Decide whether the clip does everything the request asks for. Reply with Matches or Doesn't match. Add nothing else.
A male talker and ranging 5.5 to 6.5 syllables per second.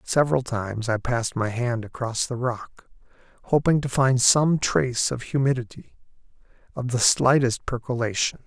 Doesn't match